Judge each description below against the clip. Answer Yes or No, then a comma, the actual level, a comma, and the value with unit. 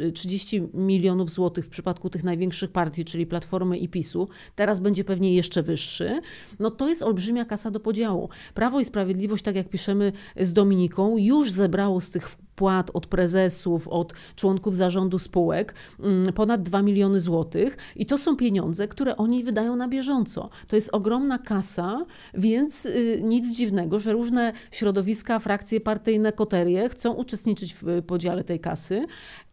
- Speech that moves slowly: No, average, 150 wpm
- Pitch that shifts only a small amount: No, average, 3.4 semitones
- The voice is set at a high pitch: Yes, high, 200 Hz